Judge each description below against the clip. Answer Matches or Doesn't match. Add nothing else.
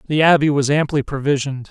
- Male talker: Matches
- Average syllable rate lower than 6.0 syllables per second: Doesn't match